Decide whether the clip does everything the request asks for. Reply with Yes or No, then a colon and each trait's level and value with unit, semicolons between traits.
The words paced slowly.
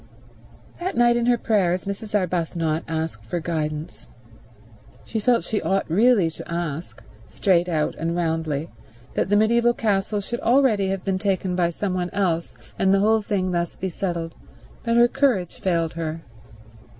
No: average, 160 wpm